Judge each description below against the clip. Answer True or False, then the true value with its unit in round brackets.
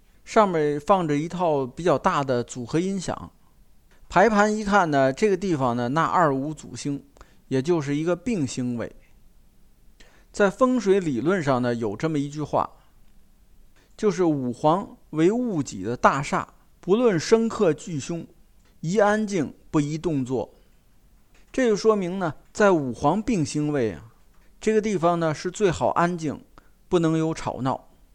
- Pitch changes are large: True (5.8 semitones)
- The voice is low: False (165 Hz)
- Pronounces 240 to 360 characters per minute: False (215 characters per minute)